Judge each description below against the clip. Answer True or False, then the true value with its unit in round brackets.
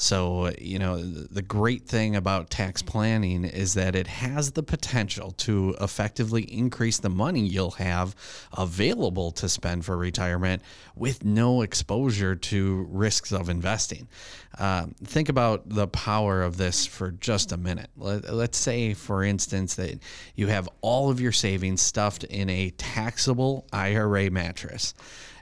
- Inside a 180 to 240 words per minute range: False (145 wpm)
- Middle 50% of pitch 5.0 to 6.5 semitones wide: False (3.1 semitones)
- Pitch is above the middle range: False (100 Hz)